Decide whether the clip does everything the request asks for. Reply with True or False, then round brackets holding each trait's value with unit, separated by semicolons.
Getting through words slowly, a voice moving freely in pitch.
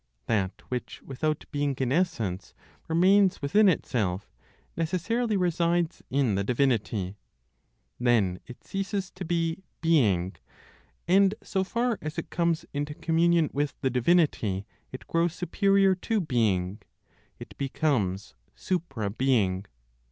True (120 wpm; 7.9 semitones)